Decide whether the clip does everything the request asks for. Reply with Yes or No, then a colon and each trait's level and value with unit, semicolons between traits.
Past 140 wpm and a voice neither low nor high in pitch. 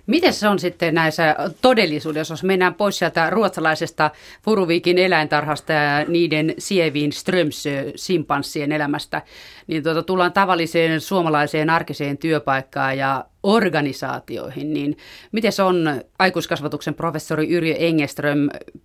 No: average, 115 wpm; medium, 160 Hz